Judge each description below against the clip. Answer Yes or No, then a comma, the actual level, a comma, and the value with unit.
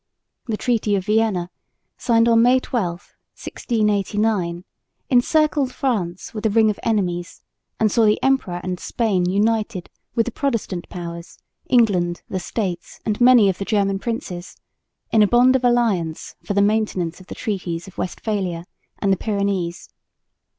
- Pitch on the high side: Yes, high, 210 Hz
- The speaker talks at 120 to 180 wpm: Yes, average, 150 wpm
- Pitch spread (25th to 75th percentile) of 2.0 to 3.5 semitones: No, average, 4.1 semitones